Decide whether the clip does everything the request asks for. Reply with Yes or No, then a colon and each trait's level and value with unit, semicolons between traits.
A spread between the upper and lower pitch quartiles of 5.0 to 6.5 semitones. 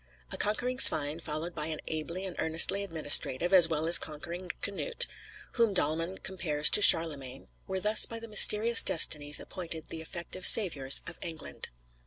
No: average, 3.9 semitones